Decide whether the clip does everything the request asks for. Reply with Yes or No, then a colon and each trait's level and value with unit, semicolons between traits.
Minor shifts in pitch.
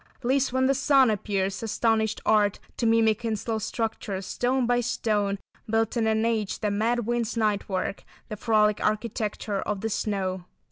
Yes: narrow, 2.2 semitones